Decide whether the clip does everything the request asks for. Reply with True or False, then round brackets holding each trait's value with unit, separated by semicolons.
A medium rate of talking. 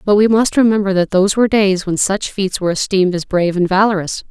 False (235 wpm)